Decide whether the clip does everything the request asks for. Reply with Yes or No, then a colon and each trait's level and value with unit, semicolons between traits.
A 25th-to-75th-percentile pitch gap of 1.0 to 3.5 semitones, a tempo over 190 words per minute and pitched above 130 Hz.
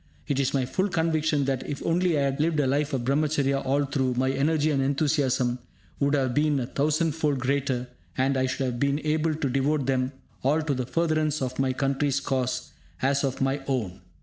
Yes: narrow, 2.4 semitones; average, 200 wpm; medium, 140 Hz